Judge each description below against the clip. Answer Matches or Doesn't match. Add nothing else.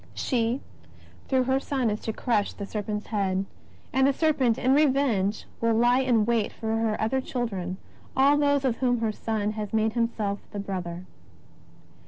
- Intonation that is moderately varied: Matches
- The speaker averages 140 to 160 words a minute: Doesn't match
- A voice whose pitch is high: Matches